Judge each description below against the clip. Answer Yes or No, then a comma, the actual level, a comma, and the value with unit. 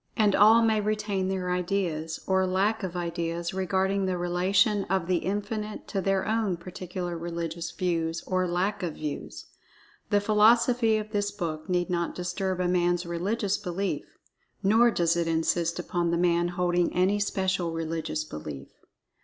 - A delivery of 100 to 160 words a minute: Yes, average, 155 wpm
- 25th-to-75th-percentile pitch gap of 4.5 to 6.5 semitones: No, average, 2.8 semitones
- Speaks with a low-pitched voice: No, medium, 185 Hz